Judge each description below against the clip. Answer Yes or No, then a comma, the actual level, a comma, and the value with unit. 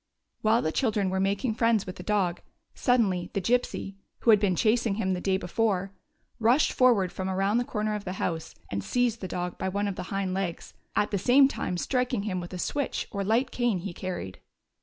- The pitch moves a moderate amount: Yes, average, 3.7 semitones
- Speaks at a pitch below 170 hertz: No, high, 200 Hz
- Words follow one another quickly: Yes, fast, 215 wpm